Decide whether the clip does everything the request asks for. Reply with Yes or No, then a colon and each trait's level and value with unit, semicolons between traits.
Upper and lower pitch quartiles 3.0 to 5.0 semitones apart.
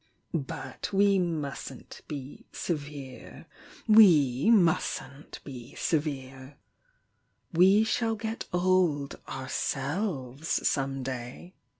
No: wide, 5.6 semitones